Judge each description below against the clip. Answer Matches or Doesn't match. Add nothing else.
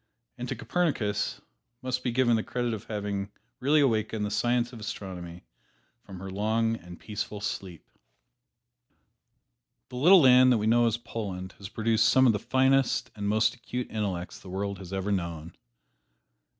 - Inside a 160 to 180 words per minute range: Matches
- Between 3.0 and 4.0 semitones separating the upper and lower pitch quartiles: Matches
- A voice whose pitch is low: Matches